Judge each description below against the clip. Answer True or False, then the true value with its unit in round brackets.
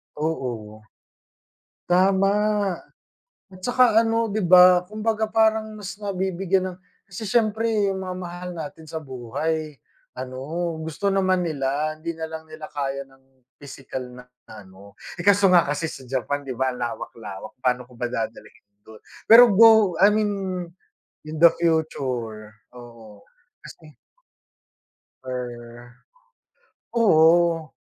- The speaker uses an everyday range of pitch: False (6.9 semitones)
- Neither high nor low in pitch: True (160 Hz)